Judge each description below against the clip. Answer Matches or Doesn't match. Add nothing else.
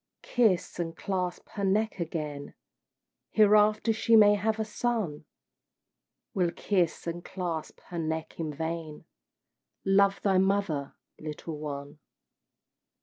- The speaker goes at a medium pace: Doesn't match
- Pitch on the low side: Doesn't match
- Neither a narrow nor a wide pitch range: Matches